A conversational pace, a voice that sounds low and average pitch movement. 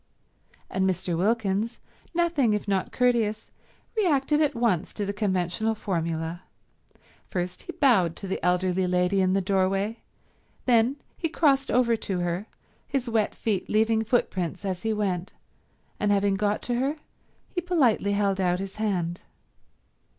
No: average, 145 wpm; high, 205 Hz; average, 4.2 semitones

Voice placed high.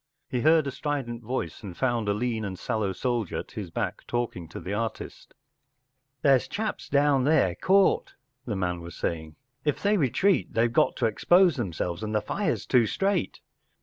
No: low, 120 Hz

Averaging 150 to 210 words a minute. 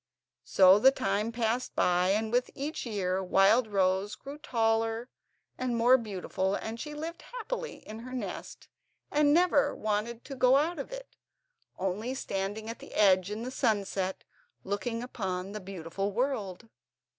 Yes: average, 155 wpm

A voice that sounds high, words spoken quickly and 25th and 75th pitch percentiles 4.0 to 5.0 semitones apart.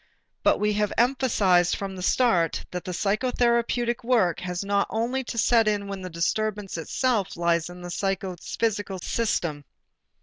No: high, 200 Hz; average, 155 wpm; average, 4.5 semitones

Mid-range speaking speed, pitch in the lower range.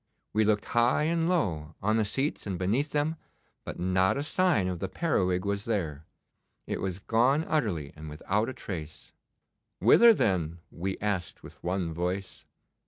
Yes: average, 165 wpm; low, 100 Hz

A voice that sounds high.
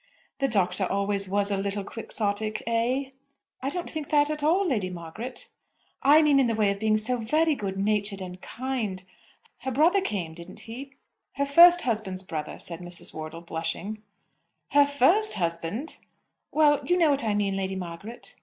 Yes: high, 215 Hz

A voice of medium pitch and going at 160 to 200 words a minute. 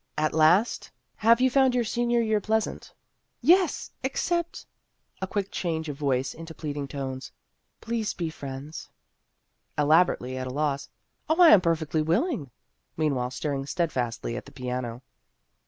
Yes: medium, 160 Hz; average, 175 wpm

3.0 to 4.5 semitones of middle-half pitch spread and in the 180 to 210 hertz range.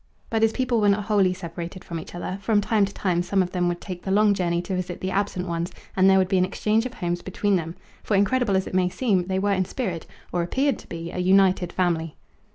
No: narrow, 2.5 semitones; high, 190 Hz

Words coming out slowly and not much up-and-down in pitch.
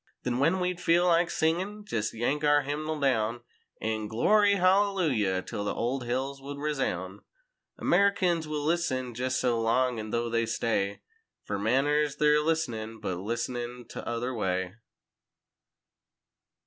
No: slow, 130 wpm; wide, 5.6 semitones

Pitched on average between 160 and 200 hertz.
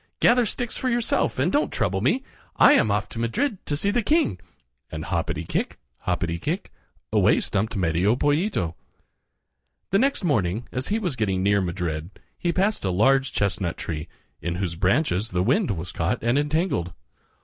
No: low, 110 Hz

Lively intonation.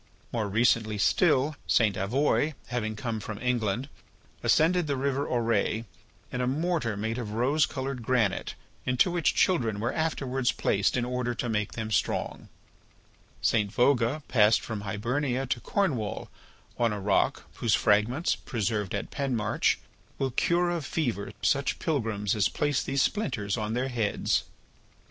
No: average, 4.3 semitones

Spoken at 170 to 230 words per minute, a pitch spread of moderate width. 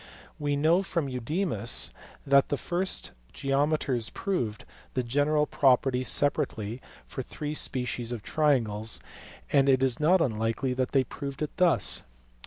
No: slow, 135 wpm; average, 3.6 semitones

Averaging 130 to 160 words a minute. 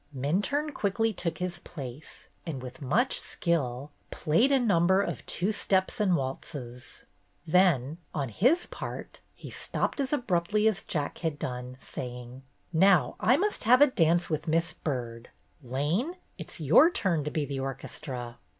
Yes: average, 150 wpm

